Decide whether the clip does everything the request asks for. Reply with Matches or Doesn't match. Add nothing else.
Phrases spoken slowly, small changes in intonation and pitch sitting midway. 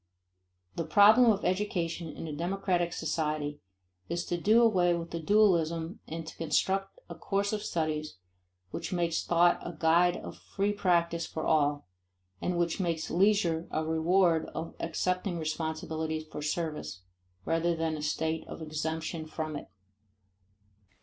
Doesn't match